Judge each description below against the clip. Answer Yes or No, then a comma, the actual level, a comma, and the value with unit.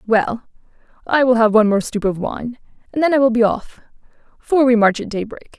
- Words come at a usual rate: No, fast, 215 wpm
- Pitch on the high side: Yes, high, 235 Hz